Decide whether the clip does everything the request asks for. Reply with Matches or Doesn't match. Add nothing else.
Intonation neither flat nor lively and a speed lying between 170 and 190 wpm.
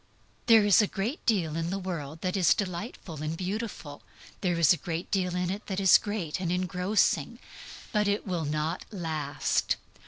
Matches